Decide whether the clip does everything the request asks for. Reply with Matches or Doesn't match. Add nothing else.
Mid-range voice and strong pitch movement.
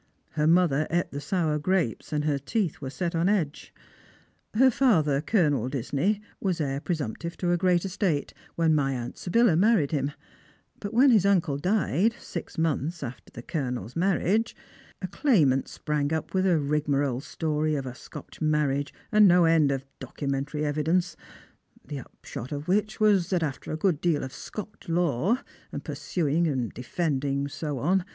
Doesn't match